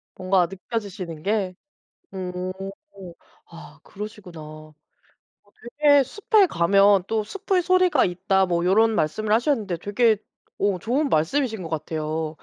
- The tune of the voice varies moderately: Yes, average, 4.8 semitones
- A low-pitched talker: No, high, 195 Hz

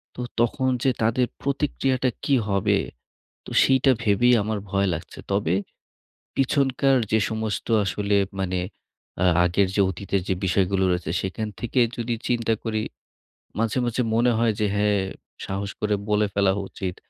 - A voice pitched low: Yes, low, 105 Hz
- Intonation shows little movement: No, average, 3.7 semitones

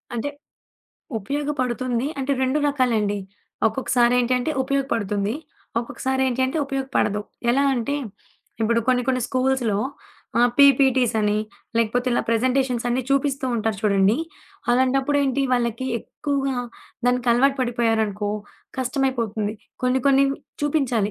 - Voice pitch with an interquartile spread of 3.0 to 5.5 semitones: No, narrow, 2.6 semitones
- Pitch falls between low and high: No, very high, 250 Hz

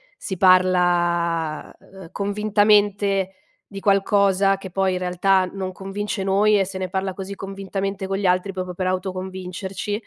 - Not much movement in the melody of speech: Yes, narrow, 1.3 semitones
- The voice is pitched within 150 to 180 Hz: No, high, 190 Hz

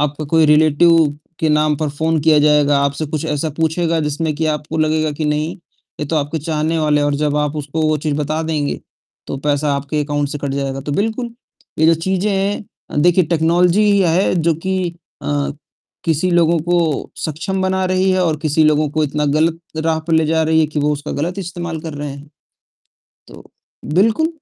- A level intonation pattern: Yes, narrow, 2.1 semitones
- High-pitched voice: No, medium, 155 Hz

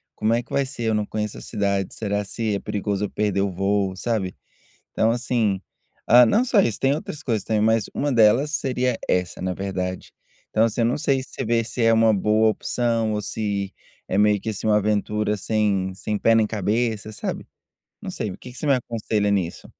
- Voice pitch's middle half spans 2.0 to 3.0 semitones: Yes, narrow, 2.4 semitones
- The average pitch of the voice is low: Yes, low, 110 Hz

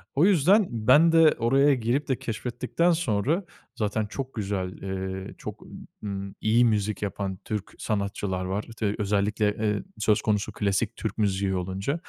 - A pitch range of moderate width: Yes, average, 4.3 semitones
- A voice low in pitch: Yes, low, 105 Hz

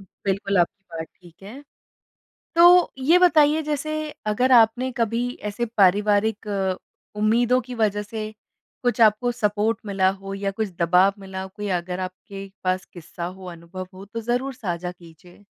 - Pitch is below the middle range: No, high, 205 Hz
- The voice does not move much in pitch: No, average, 4.2 semitones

